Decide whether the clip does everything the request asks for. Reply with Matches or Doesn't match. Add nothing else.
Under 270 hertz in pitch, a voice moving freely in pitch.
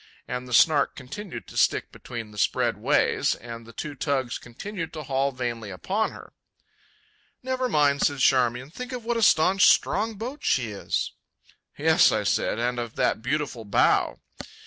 Matches